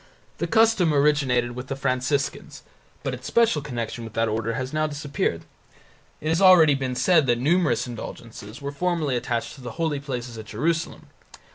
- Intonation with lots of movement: No, average, 4.4 semitones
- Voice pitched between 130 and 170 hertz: Yes, low, 135 Hz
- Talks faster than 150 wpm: Yes, average, 170 wpm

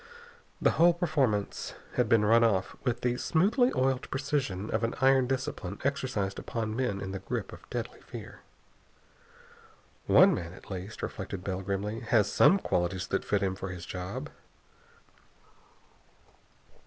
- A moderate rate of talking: Yes, average, 145 wpm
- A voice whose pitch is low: Yes, low, 110 Hz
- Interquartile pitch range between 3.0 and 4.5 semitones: No, wide, 5.4 semitones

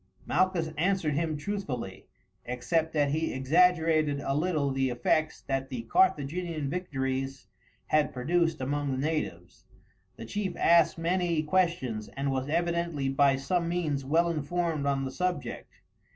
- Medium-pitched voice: Yes, medium, 155 Hz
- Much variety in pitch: No, average, 4.0 semitones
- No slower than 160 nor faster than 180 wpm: No, slow, 135 wpm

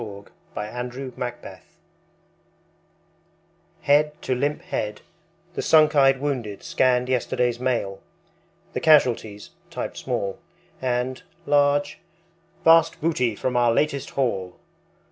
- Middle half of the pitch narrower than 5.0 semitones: Yes, average, 3.4 semitones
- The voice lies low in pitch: Yes, low, 125 Hz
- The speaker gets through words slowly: Yes, slow, 105 wpm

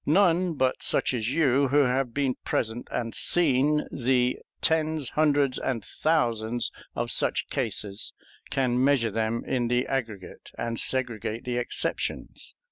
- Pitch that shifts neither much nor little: Yes, average, 3.5 semitones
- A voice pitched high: No, low, 125 Hz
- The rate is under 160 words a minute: Yes, slow, 135 wpm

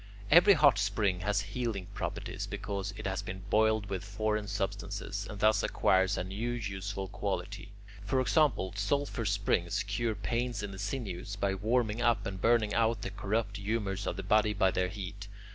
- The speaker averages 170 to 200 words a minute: Yes, average, 175 wpm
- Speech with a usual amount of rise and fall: No, narrow, 2.3 semitones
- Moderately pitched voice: No, low, 100 Hz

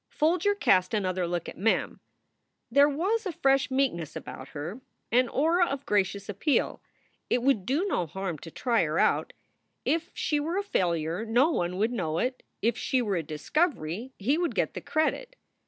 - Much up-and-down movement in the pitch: Yes, wide, 8.7 semitones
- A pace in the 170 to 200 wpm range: Yes, average, 180 wpm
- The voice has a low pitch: No, high, 240 Hz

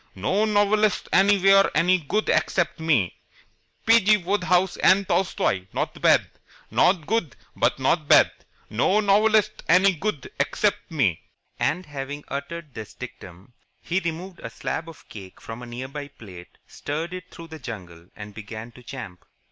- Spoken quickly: No, average, 155 wpm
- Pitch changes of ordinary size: No, wide, 8.2 semitones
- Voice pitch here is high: No, medium, 160 Hz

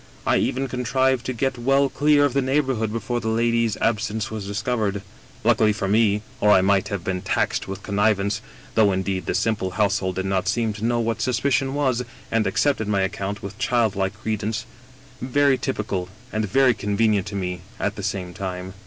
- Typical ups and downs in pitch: Yes, average, 3.8 semitones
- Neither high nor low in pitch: No, low, 110 Hz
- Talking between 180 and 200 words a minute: Yes, average, 190 wpm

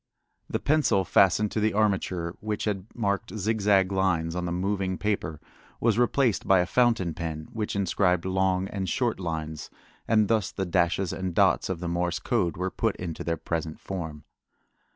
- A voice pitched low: Yes, very low, 95 Hz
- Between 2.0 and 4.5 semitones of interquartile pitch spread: Yes, average, 3.4 semitones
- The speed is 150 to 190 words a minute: Yes, average, 175 wpm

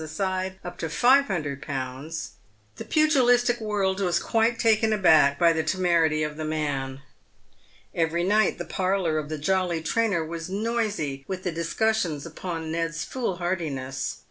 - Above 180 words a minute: No, average, 145 wpm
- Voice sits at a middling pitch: Yes, medium, 175 Hz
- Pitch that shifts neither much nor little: Yes, average, 4.6 semitones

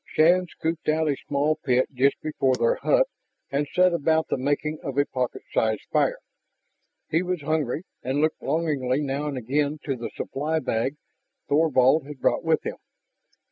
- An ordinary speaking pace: Yes, average, 170 wpm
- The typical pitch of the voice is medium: Yes, medium, 145 Hz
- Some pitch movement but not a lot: Yes, average, 3.0 semitones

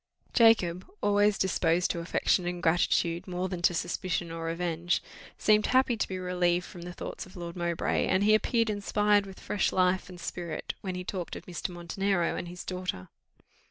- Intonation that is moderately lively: No, narrow, 2.2 semitones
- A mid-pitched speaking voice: Yes, medium, 180 Hz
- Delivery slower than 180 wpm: No, average, 185 wpm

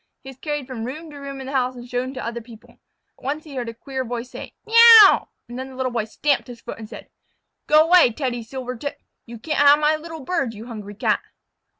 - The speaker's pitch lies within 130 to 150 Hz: No, very high, 260 Hz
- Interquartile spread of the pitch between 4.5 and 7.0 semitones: No, average, 3.7 semitones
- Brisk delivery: Yes, fast, 235 wpm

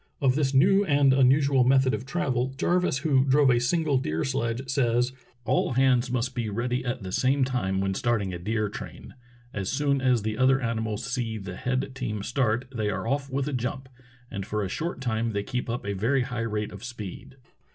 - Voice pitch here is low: Yes, low, 125 Hz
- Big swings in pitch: No, average, 3.3 semitones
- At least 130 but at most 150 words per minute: No, fast, 205 wpm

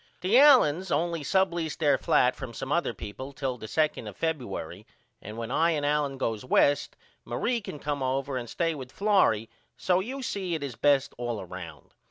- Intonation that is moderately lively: No, wide, 5.7 semitones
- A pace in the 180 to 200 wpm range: Yes, average, 190 wpm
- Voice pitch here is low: No, medium, 145 Hz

